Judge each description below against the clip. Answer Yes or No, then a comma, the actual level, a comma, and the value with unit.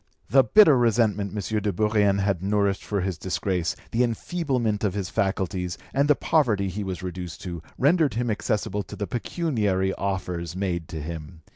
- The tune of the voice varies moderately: Yes, average, 3.8 semitones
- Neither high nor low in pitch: No, low, 100 Hz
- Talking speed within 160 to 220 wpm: Yes, average, 170 wpm